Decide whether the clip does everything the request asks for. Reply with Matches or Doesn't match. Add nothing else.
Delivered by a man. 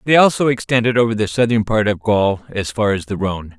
Matches